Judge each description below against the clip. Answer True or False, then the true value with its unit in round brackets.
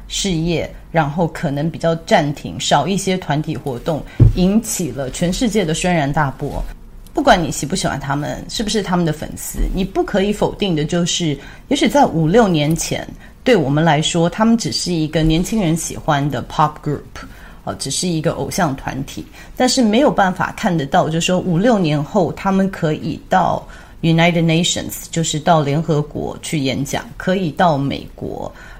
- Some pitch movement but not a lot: True (4.2 semitones)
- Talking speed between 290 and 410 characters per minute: True (300 characters per minute)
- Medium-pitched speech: True (165 Hz)